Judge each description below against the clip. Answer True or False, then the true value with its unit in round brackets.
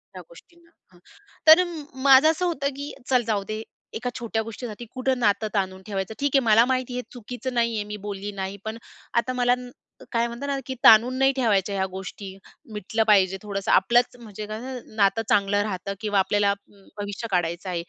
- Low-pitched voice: False (220 Hz)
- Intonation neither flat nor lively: True (3.8 semitones)